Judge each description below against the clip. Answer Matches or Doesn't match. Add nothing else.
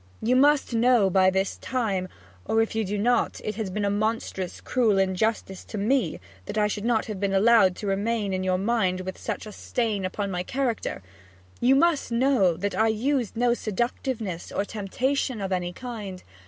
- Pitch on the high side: Matches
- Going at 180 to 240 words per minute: Matches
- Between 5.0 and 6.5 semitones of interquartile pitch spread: Doesn't match